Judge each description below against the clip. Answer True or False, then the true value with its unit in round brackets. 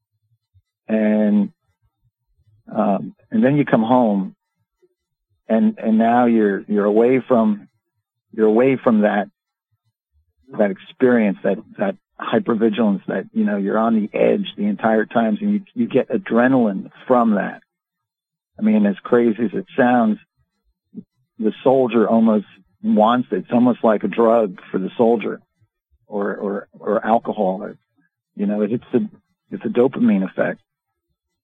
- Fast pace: False (140 wpm)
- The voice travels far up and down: True (7.4 semitones)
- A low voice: True (115 Hz)